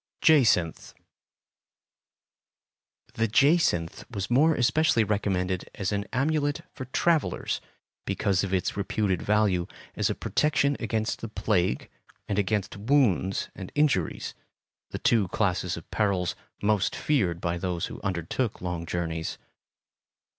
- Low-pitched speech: Yes, low, 100 Hz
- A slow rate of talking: Yes, slow, 120 wpm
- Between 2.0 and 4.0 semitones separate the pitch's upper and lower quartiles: No, wide, 5.6 semitones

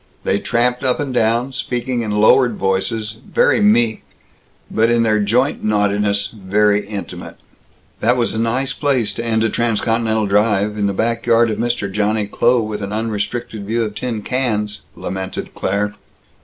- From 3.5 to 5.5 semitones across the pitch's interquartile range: No, narrow, 2.4 semitones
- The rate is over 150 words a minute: Yes, average, 165 wpm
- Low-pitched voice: Yes, low, 110 Hz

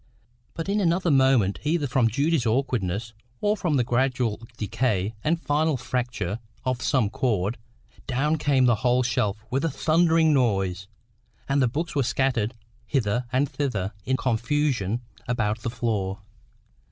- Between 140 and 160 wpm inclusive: Yes, average, 145 wpm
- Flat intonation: No, average, 4.7 semitones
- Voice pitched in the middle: No, low, 125 Hz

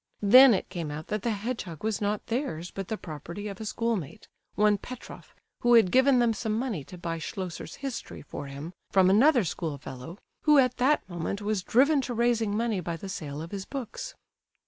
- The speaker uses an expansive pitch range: Yes, wide, 5.8 semitones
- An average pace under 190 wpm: No, average, 195 wpm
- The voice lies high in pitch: Yes, high, 205 Hz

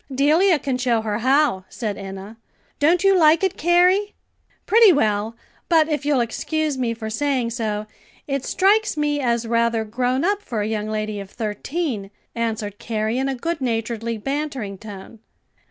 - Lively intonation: Yes, wide, 5.8 semitones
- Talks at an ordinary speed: Yes, average, 165 wpm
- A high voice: Yes, high, 245 Hz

